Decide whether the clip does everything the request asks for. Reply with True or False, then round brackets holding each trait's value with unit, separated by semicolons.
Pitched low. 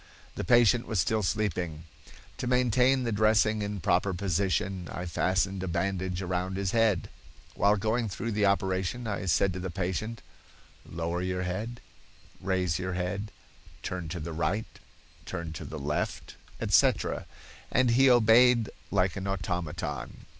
True (95 Hz)